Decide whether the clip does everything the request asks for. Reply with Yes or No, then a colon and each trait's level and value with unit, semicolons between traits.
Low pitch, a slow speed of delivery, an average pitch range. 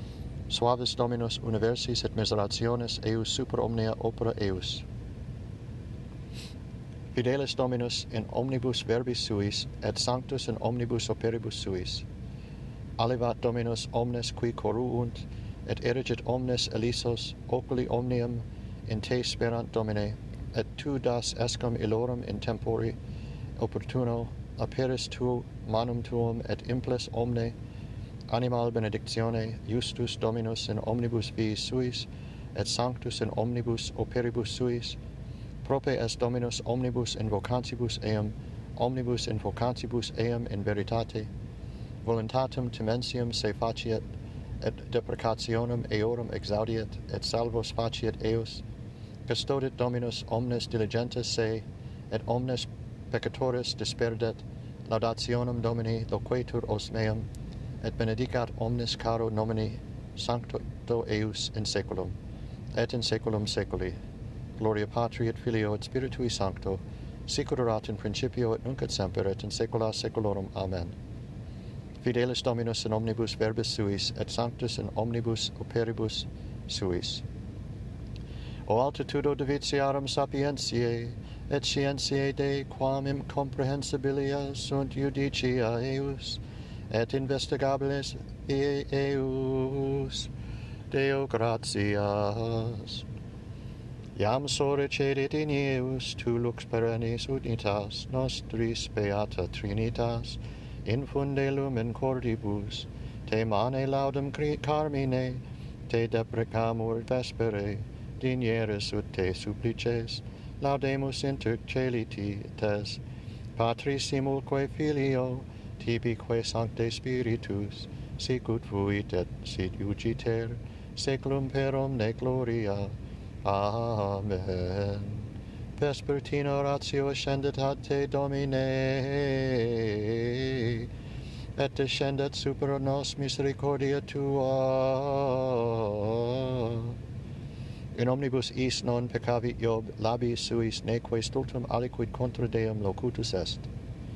No: low, 115 Hz; slow, 100 wpm; narrow, 2.2 semitones